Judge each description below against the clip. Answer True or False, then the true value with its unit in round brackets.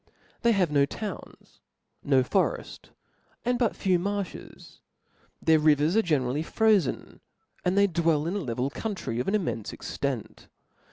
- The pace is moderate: True (145 wpm)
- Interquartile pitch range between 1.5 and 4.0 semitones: False (5.6 semitones)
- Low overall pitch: False (170 Hz)